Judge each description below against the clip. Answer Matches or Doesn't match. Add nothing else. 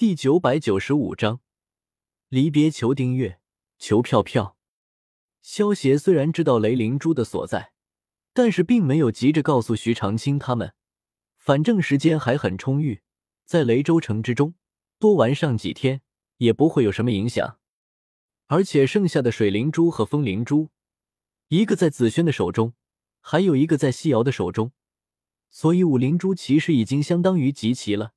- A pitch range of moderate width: Doesn't match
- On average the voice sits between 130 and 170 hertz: Matches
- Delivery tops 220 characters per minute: Matches